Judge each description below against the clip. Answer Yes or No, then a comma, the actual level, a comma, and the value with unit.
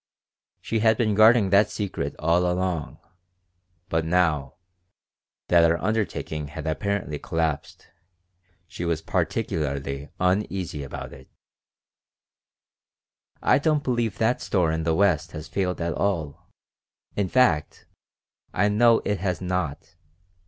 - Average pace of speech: No, slow, 120 wpm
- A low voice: Yes, very low, 90 Hz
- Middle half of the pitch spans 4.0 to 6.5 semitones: Yes, average, 4.5 semitones